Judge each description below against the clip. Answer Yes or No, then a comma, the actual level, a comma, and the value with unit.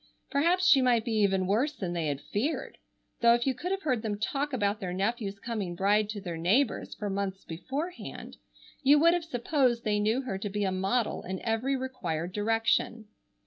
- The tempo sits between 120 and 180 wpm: No, average, 195 wpm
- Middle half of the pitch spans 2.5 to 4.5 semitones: No, average, 5.0 semitones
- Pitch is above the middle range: Yes, high, 225 Hz